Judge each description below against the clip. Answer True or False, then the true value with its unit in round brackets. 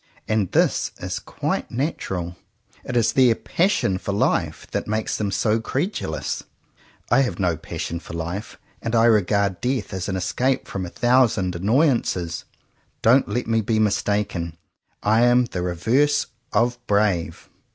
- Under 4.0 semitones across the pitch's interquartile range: False (4.7 semitones)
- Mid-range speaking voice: False (110 Hz)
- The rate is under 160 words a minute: True (150 wpm)